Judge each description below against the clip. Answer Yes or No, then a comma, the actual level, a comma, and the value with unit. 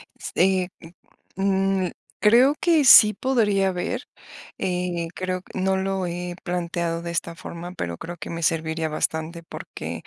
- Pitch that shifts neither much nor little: No, narrow, 2.3 semitones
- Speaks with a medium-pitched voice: Yes, medium, 180 Hz